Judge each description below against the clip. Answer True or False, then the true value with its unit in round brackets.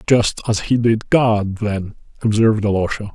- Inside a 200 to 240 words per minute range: False (150 wpm)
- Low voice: True (110 Hz)